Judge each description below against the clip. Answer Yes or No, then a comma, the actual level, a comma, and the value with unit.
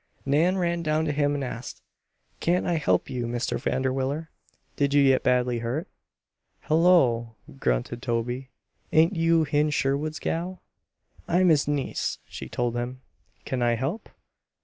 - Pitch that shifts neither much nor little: Yes, average, 4.7 semitones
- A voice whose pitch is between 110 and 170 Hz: Yes, medium, 140 Hz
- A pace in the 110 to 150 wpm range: Yes, average, 145 wpm